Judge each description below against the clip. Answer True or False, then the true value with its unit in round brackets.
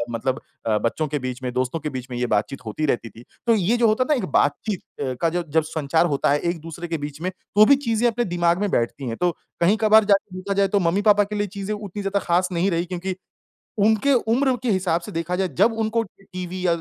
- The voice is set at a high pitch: False (180 Hz)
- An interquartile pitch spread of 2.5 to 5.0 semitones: False (5.5 semitones)